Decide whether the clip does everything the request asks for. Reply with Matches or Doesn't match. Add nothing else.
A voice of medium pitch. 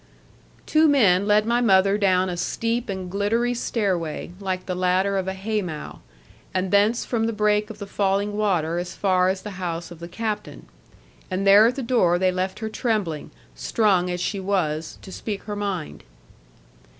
Doesn't match